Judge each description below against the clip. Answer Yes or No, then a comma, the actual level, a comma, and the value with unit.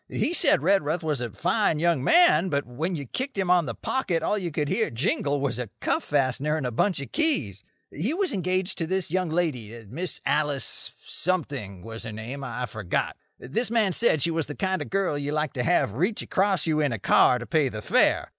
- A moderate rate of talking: No, fast, 220 wpm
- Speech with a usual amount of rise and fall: No, wide, 6.4 semitones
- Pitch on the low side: No, medium, 155 Hz